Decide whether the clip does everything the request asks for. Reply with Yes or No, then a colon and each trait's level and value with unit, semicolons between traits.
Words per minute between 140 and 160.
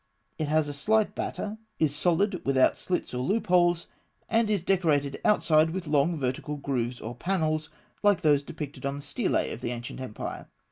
No: average, 175 wpm